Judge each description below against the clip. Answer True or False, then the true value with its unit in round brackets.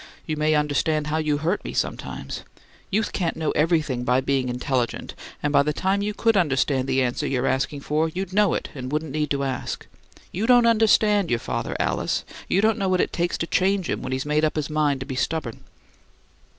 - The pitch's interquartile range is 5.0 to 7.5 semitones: True (5.3 semitones)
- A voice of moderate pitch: True (155 Hz)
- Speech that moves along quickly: True (215 wpm)